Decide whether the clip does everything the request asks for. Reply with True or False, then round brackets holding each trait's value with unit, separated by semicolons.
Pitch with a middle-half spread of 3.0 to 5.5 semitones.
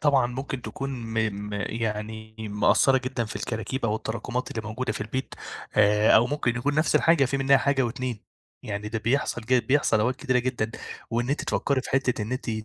True (3.4 semitones)